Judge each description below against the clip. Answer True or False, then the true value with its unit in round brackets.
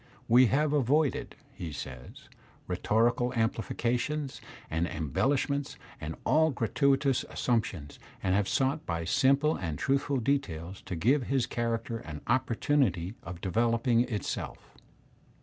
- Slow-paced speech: True (125 wpm)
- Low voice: True (120 Hz)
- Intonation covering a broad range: True (6.9 semitones)